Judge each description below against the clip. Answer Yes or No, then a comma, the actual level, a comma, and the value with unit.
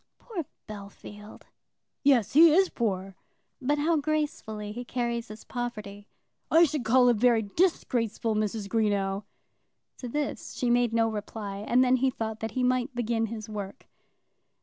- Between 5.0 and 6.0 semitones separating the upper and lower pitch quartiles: No, average, 3.4 semitones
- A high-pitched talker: Yes, high, 235 Hz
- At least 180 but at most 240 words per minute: No, average, 150 wpm